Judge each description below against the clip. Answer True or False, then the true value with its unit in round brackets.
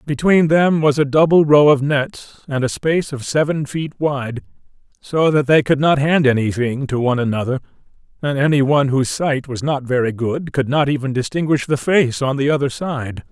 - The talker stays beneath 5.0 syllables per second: False (5.1 syllables/s)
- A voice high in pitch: False (140 Hz)